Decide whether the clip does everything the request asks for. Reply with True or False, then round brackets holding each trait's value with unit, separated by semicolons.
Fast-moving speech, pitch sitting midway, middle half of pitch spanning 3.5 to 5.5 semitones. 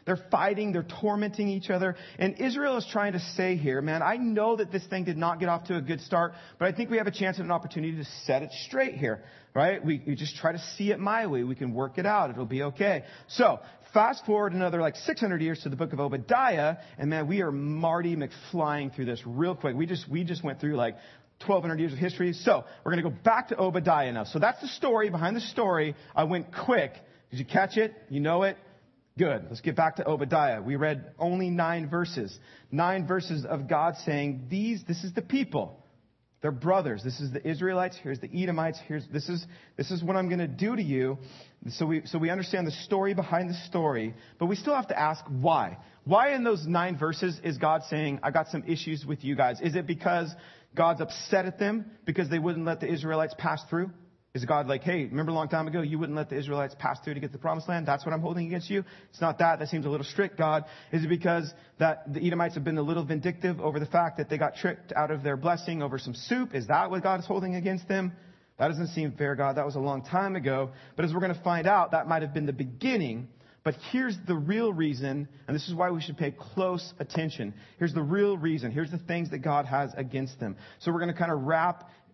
True (245 wpm; 165 Hz; 3.8 semitones)